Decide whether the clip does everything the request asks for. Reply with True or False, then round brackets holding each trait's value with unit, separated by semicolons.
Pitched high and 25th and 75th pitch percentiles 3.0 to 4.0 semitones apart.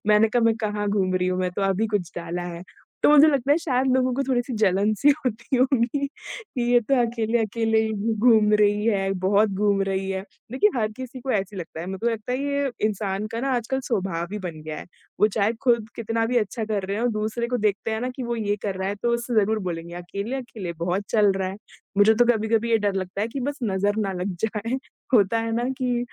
True (215 Hz; 3.5 semitones)